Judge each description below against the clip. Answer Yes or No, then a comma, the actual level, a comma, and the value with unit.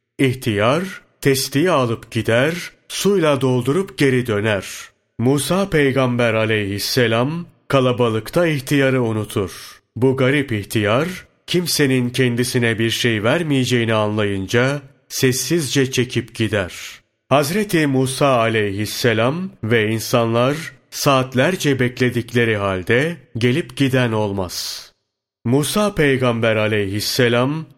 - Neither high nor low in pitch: No, low, 125 Hz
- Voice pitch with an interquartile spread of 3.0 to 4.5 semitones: Yes, average, 3.7 semitones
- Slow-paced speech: Yes, slow, 85 wpm